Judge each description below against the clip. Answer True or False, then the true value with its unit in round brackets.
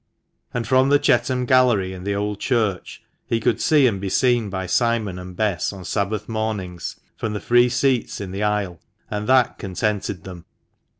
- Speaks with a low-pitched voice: True (105 Hz)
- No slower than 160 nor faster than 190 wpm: True (180 wpm)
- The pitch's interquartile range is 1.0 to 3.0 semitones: False (4.2 semitones)